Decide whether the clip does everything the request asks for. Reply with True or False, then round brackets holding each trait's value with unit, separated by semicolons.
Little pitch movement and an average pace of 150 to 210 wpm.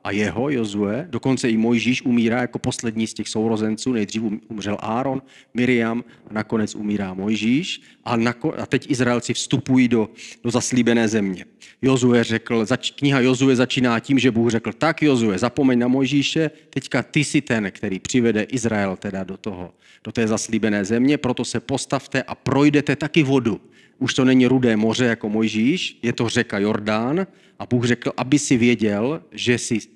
False (3.1 semitones; 165 wpm)